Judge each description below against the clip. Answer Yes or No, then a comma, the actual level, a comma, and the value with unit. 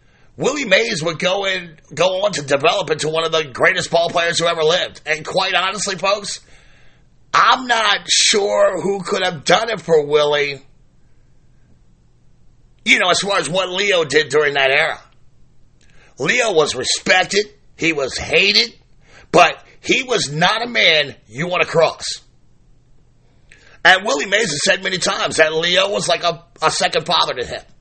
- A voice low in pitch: No, medium, 175 Hz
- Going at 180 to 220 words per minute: No, average, 165 wpm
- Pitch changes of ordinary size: Yes, average, 3.9 semitones